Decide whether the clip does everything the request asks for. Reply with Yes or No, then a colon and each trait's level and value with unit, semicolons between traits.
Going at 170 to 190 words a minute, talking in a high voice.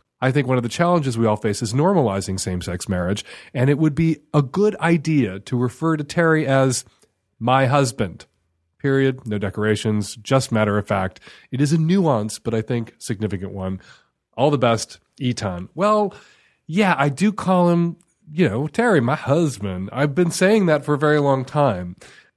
No: average, 180 wpm; low, 135 Hz